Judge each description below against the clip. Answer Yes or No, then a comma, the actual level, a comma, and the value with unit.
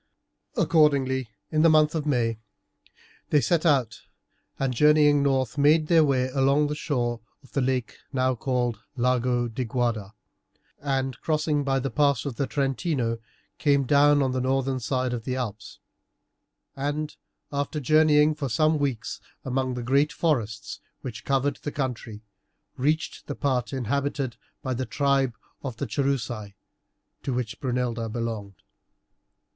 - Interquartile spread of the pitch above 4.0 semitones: No, average, 3.0 semitones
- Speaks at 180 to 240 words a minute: No, average, 145 wpm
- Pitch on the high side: No, low, 135 Hz